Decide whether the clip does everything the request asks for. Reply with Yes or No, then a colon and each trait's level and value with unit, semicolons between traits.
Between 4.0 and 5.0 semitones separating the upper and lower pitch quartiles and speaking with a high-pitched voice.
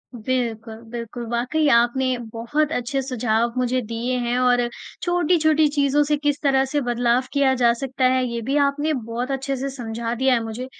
No: average, 2.9 semitones; very high, 255 Hz